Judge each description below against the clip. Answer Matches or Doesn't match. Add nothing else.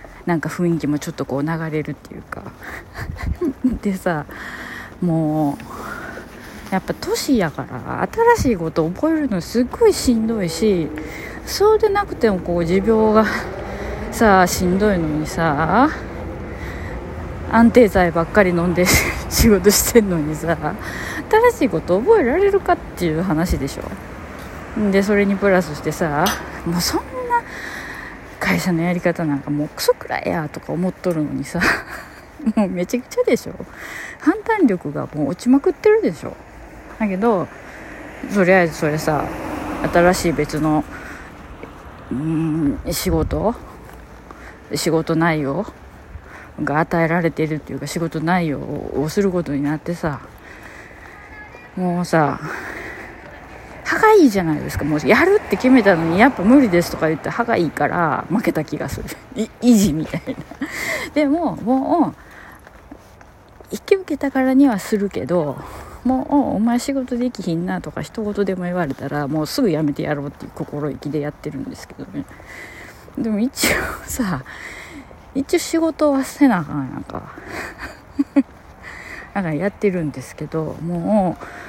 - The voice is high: Doesn't match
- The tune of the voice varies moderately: Doesn't match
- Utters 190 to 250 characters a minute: Doesn't match